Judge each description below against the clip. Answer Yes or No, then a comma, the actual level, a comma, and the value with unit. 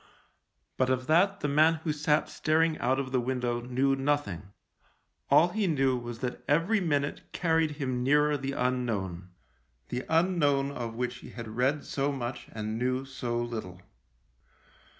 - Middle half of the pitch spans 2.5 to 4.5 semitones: Yes, average, 3.7 semitones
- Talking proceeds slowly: No, average, 160 wpm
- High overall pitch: No, low, 130 Hz